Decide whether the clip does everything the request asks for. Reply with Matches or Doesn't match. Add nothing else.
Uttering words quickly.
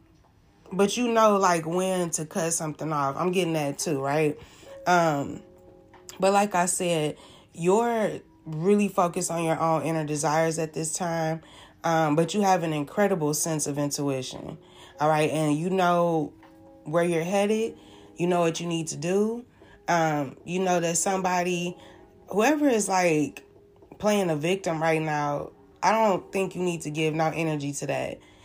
Doesn't match